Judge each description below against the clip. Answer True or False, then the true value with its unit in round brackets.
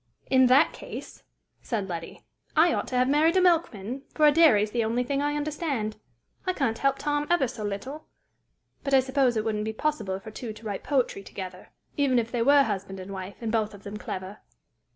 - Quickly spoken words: True (215 wpm)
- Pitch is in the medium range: False (245 Hz)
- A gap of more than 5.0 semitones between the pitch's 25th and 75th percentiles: True (5.4 semitones)